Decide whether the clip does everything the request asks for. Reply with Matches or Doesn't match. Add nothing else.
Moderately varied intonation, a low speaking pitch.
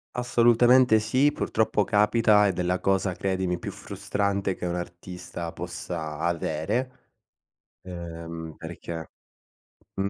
Matches